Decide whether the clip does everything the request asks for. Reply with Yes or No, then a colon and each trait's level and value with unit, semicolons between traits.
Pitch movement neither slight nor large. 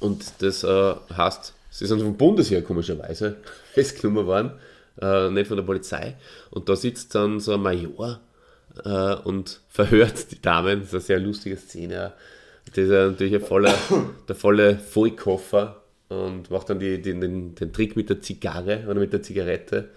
No: narrow, 1.5 semitones